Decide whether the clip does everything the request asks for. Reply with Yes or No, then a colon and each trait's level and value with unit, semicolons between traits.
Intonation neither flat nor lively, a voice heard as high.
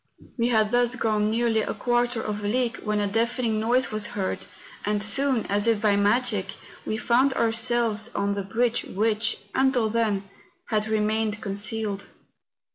No: narrow, 2.3 semitones; high, 220 Hz